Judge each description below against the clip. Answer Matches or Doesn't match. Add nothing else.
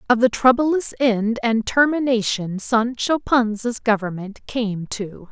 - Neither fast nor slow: Doesn't match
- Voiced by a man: Doesn't match